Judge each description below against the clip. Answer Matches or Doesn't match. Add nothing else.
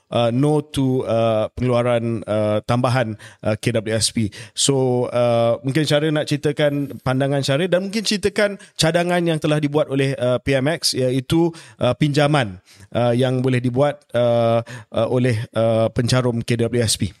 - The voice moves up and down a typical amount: Matches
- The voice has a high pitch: Doesn't match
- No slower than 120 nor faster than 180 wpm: Matches